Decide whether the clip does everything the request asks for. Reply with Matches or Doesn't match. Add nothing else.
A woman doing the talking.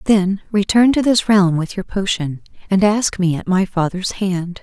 Matches